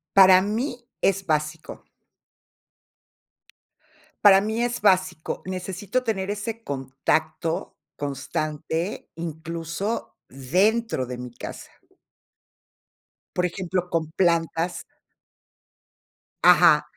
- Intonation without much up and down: No, average, 4.4 semitones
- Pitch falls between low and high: Yes, medium, 180 Hz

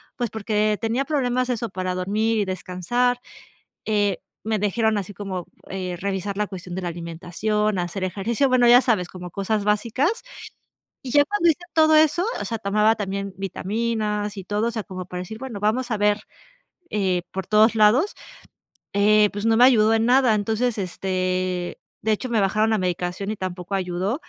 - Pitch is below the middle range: No, high, 210 Hz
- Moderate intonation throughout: Yes, average, 3.4 semitones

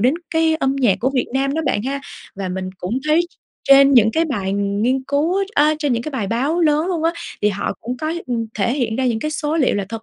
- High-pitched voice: Yes, very high, 260 Hz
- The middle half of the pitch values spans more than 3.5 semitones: Yes, wide, 5.5 semitones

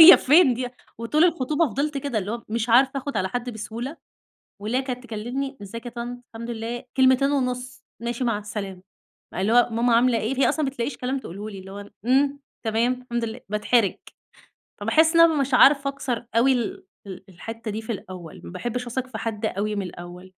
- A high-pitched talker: Yes, high, 240 Hz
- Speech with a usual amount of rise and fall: Yes, average, 3.5 semitones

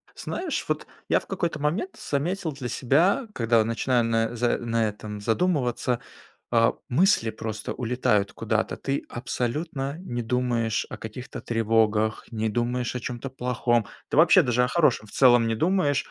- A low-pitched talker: Yes, low, 120 Hz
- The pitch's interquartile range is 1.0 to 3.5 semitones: No, average, 3.9 semitones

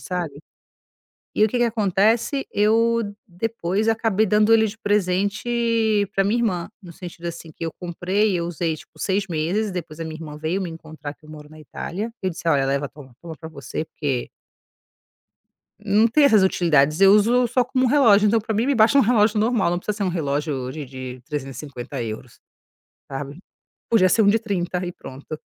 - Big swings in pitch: Yes, wide, 5.7 semitones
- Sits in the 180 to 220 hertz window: Yes, medium, 185 Hz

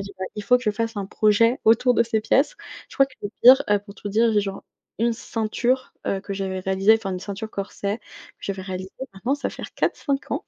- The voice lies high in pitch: Yes, high, 210 Hz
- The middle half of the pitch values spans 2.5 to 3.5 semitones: Yes, average, 2.9 semitones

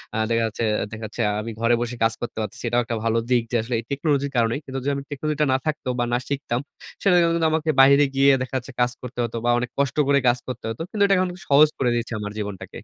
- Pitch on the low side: Yes, low, 125 Hz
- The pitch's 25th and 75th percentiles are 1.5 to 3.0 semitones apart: No, average, 3.4 semitones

